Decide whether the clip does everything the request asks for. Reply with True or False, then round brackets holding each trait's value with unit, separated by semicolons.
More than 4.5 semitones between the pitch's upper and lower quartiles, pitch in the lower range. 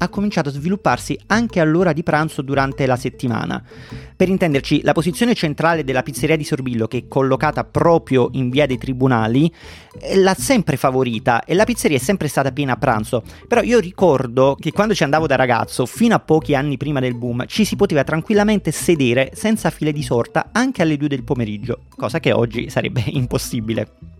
False (5.0 semitones; 145 Hz)